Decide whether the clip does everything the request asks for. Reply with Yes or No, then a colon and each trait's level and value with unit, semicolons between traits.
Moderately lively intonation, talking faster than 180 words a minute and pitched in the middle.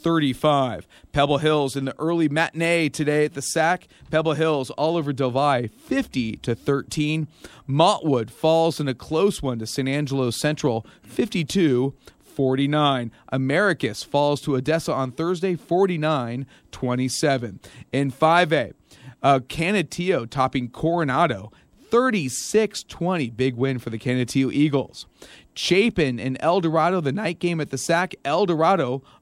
No: average, 4.0 semitones; slow, 135 wpm; medium, 145 Hz